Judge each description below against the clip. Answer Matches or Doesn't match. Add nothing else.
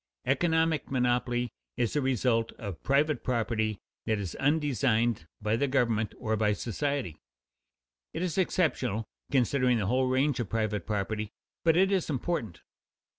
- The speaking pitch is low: Matches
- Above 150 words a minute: Doesn't match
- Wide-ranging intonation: Doesn't match